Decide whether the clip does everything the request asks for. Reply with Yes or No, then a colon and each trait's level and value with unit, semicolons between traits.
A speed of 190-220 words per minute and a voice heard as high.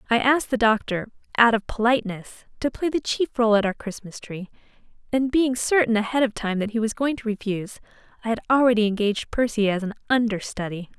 Yes: average, 195 wpm; high, 225 Hz